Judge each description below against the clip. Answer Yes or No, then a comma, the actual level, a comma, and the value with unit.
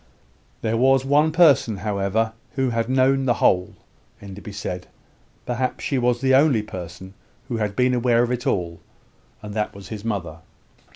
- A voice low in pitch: Yes, low, 115 Hz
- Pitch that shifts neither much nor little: Yes, average, 4.4 semitones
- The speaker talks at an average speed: Yes, average, 165 wpm